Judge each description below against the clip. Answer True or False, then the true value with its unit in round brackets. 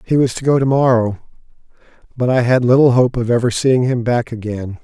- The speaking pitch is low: True (125 Hz)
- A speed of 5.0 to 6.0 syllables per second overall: True (5.4 syllables/s)